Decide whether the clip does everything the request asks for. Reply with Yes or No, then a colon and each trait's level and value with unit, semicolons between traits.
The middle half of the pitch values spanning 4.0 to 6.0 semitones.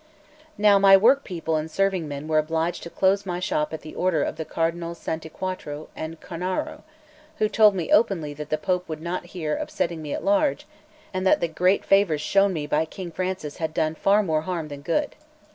No: average, 3.6 semitones